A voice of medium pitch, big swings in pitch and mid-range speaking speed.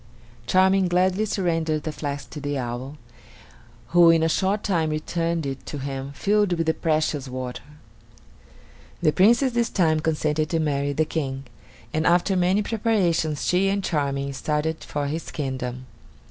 No: medium, 160 Hz; average, 4.2 semitones; average, 155 wpm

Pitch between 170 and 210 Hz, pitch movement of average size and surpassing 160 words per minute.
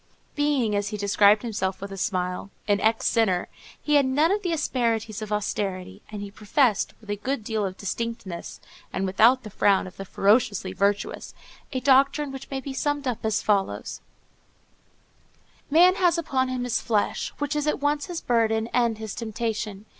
No: high, 220 Hz; average, 4.8 semitones; average, 180 wpm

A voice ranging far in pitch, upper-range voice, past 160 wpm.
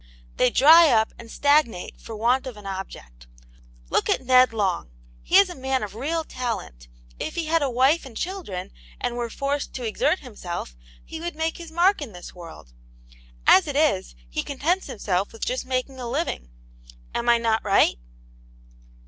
Yes: wide, 6.4 semitones; very high, 250 Hz; average, 180 wpm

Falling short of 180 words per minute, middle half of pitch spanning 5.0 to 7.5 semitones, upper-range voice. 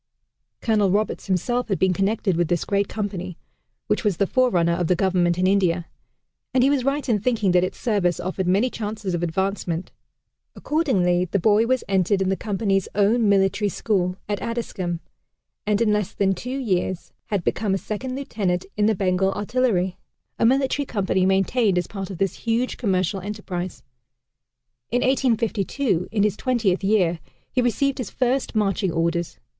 No: average, 170 wpm; average, 3.8 semitones; high, 200 Hz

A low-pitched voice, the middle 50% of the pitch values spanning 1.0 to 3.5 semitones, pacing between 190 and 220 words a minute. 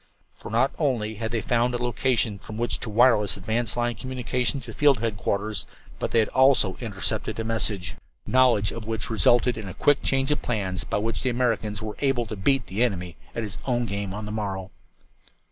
Yes: low, 115 Hz; average, 2.9 semitones; average, 200 wpm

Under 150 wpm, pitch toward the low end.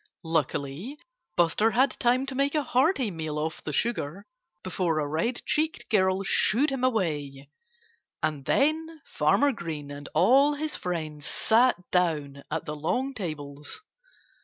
No: average, 140 wpm; medium, 180 Hz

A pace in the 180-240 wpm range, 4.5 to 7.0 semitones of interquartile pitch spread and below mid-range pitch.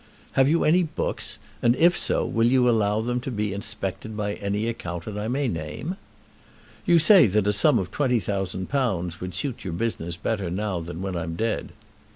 Yes: average, 185 wpm; average, 4.9 semitones; low, 105 Hz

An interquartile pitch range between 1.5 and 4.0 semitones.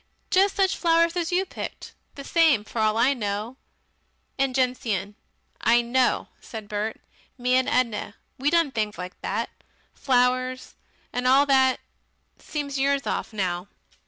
No: average, 4.4 semitones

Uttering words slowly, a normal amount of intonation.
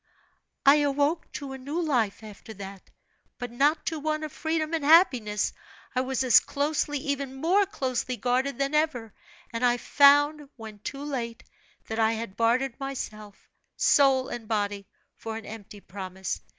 No: average, 160 wpm; average, 4.6 semitones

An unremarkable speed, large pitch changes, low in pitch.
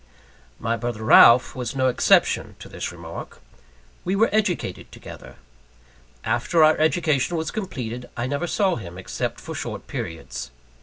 Yes: average, 145 wpm; wide, 6.8 semitones; low, 130 Hz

